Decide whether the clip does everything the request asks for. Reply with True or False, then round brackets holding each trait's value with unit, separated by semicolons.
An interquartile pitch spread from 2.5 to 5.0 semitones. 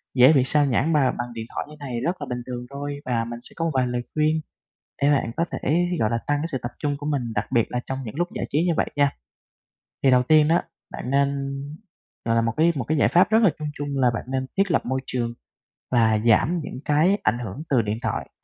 True (3.8 semitones)